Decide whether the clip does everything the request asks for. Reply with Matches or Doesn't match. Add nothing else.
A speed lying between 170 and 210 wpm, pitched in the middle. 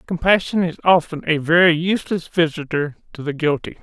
Doesn't match